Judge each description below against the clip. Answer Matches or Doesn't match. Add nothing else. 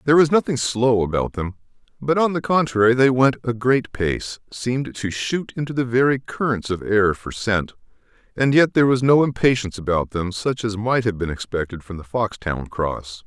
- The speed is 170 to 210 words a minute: Matches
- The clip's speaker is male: Matches